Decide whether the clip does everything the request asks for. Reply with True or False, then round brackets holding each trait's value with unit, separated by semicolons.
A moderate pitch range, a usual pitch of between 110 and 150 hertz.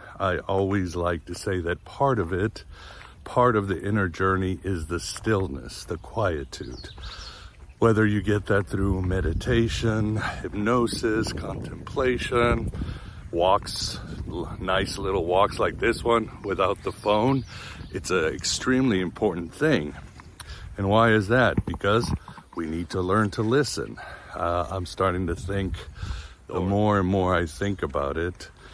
False (3.8 semitones; 95 Hz)